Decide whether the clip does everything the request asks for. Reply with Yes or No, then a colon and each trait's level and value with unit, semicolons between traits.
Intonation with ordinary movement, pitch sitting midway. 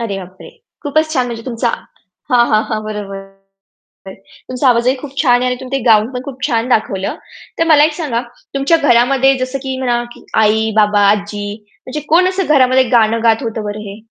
No: average, 3.9 semitones; high, 240 Hz